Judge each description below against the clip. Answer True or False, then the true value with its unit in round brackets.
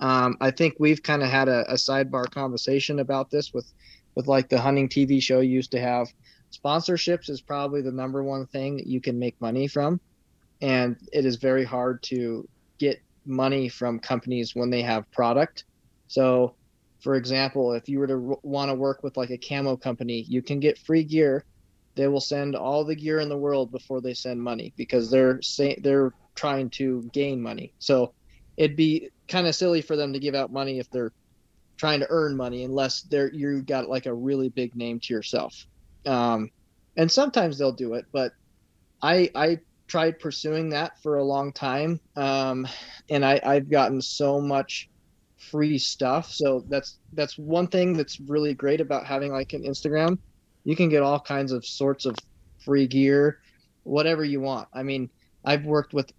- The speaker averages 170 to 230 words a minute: True (190 wpm)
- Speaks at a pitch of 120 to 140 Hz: True (135 Hz)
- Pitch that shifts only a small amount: True (2.3 semitones)